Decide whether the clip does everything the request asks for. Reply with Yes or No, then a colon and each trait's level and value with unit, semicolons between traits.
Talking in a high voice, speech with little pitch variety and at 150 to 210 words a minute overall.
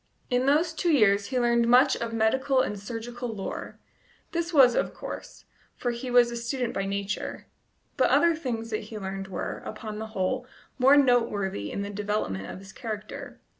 No: high, 230 Hz; average, 3.8 semitones; average, 180 wpm